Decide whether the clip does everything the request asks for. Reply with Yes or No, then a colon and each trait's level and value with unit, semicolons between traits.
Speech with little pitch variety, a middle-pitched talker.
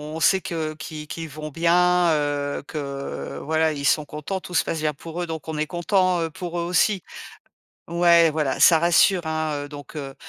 Yes: narrow, 2.3 semitones; medium, 160 Hz